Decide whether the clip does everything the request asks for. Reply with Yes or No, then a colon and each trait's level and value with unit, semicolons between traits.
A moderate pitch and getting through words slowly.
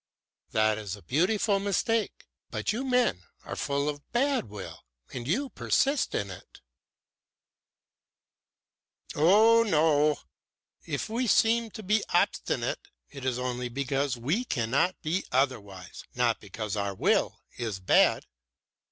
Yes: medium, 145 Hz; slow, 125 wpm